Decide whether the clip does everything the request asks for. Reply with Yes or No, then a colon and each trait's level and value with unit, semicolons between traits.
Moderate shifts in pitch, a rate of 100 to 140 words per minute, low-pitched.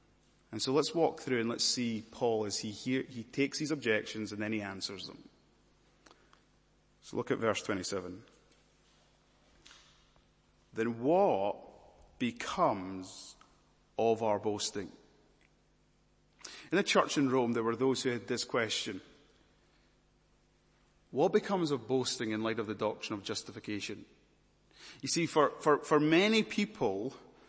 Yes: average, 4.7 semitones; slow, 135 wpm; low, 115 Hz